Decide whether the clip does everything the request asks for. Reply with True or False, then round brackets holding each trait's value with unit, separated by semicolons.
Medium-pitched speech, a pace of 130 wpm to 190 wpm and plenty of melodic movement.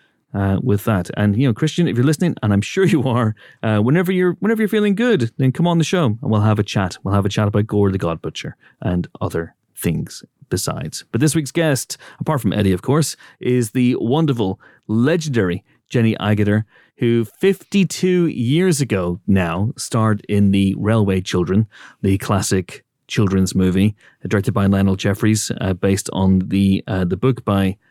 False (110 Hz; 185 wpm; 5.9 semitones)